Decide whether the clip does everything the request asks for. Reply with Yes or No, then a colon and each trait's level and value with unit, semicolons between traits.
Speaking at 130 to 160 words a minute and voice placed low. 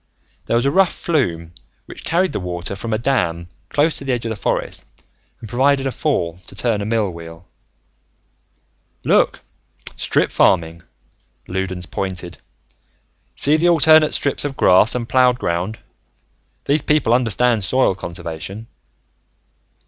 Yes: average, 140 wpm; low, 115 Hz